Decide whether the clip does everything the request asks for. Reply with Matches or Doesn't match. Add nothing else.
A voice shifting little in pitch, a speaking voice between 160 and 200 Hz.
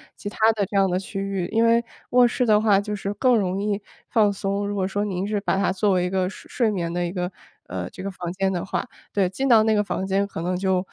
Matches